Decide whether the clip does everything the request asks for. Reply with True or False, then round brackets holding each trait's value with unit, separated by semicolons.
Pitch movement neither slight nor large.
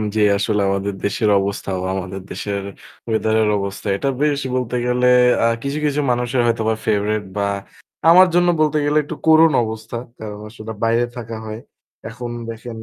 True (3.3 semitones)